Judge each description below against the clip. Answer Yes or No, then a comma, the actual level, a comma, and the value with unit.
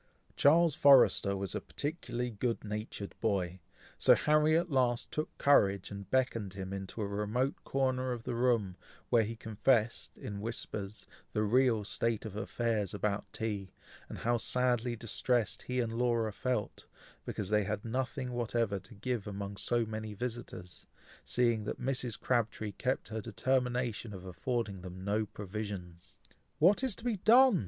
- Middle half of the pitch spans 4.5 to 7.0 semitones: No, average, 3.7 semitones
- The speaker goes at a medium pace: Yes, average, 155 wpm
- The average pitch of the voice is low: Yes, low, 115 Hz